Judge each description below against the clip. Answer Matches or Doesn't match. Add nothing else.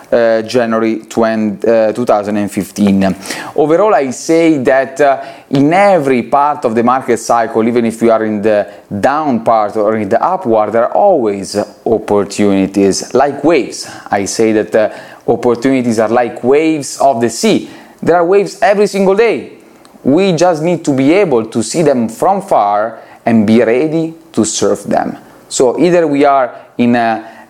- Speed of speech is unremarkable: Matches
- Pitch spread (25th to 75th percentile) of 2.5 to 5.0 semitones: Matches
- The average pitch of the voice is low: Matches